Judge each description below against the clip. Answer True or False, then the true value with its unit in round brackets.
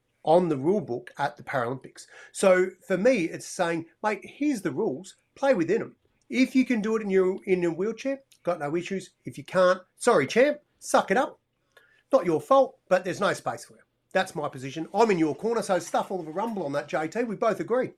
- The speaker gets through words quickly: True (225 wpm)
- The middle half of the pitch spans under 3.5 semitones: False (5.3 semitones)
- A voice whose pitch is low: False (190 Hz)